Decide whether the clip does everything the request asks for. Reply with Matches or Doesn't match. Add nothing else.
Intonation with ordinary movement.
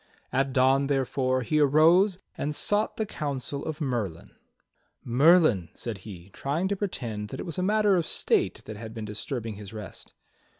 Doesn't match